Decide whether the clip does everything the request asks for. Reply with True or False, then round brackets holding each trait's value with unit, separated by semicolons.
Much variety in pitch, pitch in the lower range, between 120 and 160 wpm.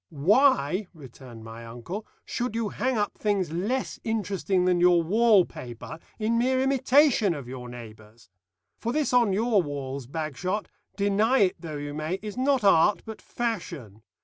False (7.8 semitones; 190 Hz; 155 wpm)